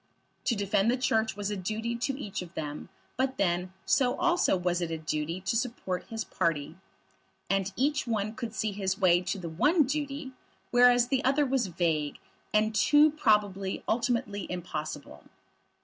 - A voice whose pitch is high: Yes, high, 215 Hz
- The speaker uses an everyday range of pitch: No, wide, 5.8 semitones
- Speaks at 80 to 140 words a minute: No, average, 165 wpm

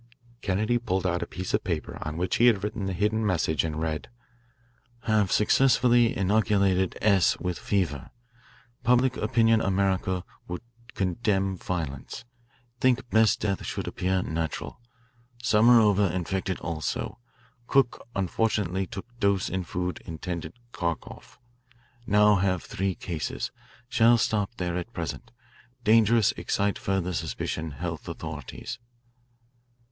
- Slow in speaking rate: Yes, slow, 120 wpm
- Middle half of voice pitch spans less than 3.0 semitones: No, average, 3.5 semitones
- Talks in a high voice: No, very low, 95 Hz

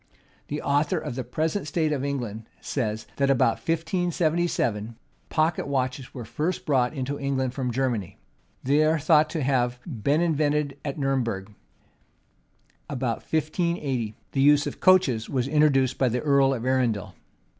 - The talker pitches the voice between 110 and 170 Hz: Yes, medium, 140 Hz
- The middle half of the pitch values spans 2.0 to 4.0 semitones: Yes, average, 3.6 semitones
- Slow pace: No, average, 150 wpm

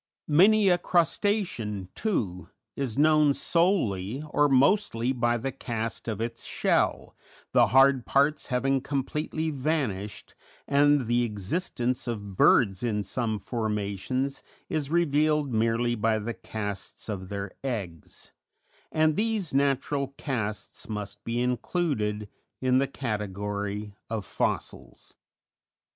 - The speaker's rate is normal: No, slow, 115 wpm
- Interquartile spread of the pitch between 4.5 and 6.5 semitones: Yes, wide, 5.5 semitones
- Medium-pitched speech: No, low, 125 Hz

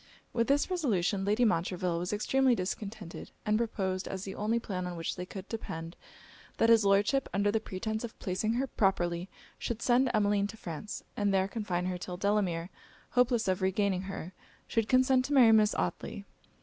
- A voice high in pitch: Yes, high, 205 Hz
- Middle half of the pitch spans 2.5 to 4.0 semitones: Yes, average, 3.6 semitones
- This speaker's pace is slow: No, average, 175 wpm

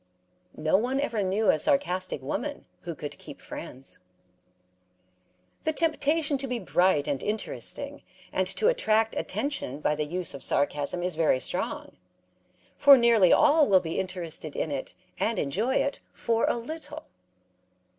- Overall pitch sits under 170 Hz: No, high, 195 Hz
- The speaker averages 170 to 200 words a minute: No, average, 145 wpm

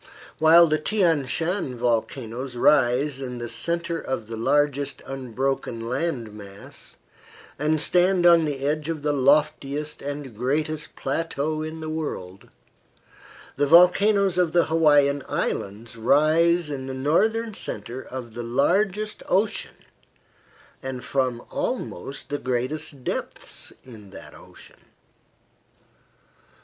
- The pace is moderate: No, slow, 120 wpm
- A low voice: No, medium, 145 Hz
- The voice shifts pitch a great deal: No, average, 4.3 semitones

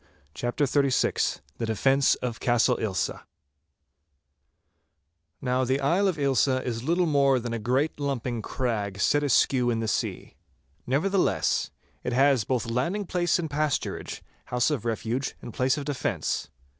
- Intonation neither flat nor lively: Yes, average, 3.3 semitones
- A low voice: Yes, low, 130 Hz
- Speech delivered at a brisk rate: No, average, 145 wpm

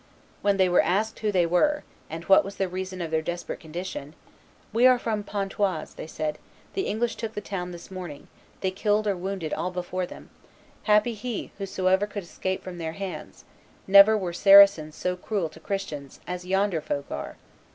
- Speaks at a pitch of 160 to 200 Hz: Yes, high, 190 Hz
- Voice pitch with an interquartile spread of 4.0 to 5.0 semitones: No, average, 2.8 semitones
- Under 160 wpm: No, average, 185 wpm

